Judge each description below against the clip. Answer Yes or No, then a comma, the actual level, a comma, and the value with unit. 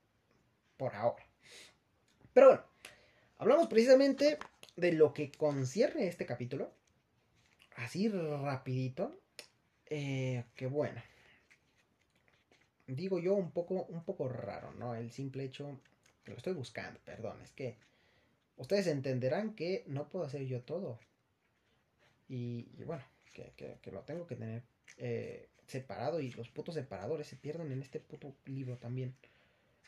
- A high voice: No, low, 135 Hz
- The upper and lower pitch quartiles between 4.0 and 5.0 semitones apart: Yes, average, 4.6 semitones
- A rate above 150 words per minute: No, average, 135 wpm